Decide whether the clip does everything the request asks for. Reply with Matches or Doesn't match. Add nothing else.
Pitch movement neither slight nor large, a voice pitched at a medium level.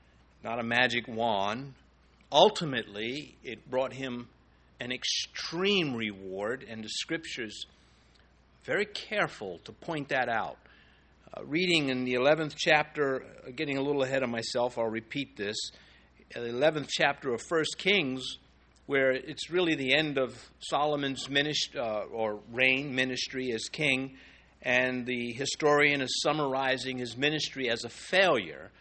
Doesn't match